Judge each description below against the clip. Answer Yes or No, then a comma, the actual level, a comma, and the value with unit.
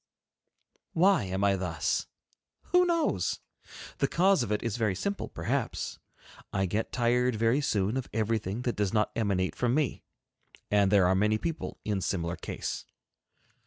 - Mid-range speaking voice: No, low, 110 Hz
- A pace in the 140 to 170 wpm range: Yes, average, 155 wpm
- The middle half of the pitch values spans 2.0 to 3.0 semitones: No, average, 4.5 semitones